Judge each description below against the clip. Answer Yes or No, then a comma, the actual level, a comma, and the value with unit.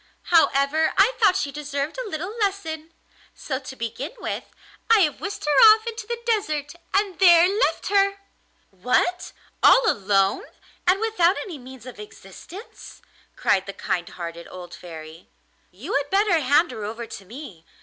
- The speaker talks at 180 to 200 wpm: No, average, 160 wpm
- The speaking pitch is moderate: No, very high, 305 Hz